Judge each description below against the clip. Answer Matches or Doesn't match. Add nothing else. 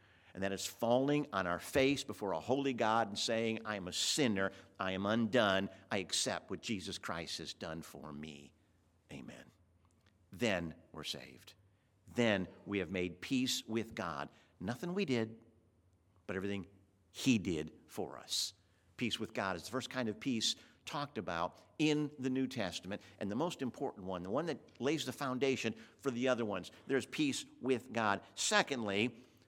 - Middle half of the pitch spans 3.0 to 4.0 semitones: Doesn't match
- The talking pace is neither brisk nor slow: Matches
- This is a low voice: Matches